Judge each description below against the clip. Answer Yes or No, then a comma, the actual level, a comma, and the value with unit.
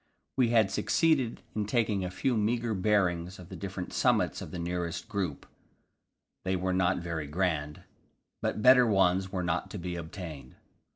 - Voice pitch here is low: Yes, very low, 95 Hz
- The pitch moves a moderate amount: Yes, average, 3.6 semitones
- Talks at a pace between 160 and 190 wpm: Yes, average, 165 wpm